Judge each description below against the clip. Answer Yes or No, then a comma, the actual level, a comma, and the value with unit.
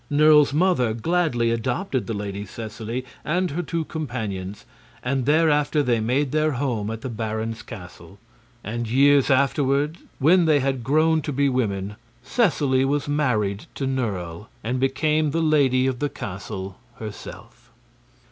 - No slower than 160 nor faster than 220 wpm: No, average, 145 wpm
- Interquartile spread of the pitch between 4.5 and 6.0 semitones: Yes, average, 5.0 semitones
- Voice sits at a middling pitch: No, low, 130 Hz